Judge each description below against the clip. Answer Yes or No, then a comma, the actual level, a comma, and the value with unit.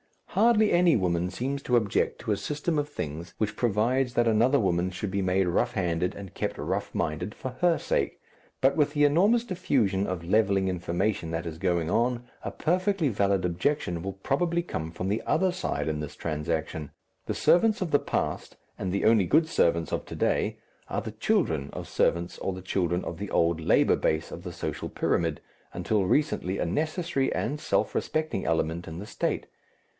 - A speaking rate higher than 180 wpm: Yes, average, 190 wpm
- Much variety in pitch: Yes, wide, 8.8 semitones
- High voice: No, low, 100 Hz